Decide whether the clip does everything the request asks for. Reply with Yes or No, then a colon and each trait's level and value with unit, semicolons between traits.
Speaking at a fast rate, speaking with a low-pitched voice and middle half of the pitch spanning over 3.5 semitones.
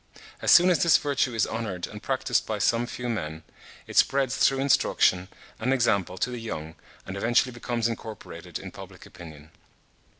No: average, 170 wpm; low, 115 Hz; wide, 5.4 semitones